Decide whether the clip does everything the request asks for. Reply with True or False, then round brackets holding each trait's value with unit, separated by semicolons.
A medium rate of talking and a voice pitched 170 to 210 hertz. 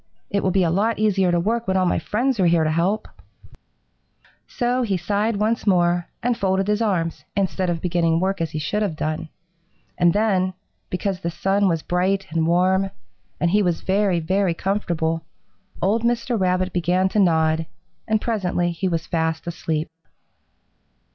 True (175 wpm; 185 Hz)